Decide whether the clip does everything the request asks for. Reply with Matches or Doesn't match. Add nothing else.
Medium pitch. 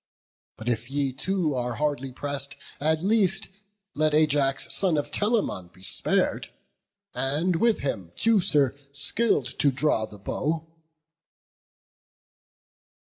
Matches